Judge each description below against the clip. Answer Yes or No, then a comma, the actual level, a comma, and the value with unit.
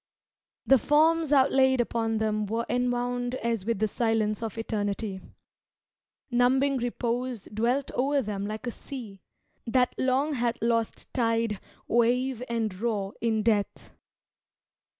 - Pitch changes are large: No, average, 2.7 semitones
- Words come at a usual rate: No, slow, 125 wpm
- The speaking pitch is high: Yes, high, 235 Hz